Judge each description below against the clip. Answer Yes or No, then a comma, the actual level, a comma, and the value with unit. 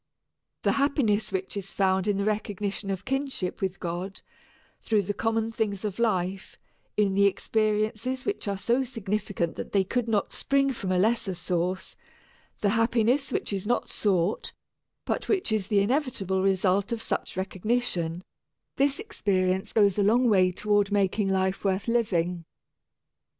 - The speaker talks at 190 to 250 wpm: No, average, 155 wpm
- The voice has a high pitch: Yes, high, 205 Hz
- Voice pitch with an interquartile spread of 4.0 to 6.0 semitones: No, average, 3.1 semitones